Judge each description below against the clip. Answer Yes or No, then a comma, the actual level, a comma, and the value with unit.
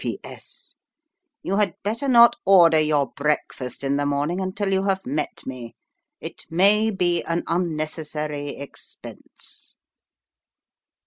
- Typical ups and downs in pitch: Yes, average, 5.0 semitones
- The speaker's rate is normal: No, slow, 125 wpm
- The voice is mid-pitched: Yes, medium, 165 Hz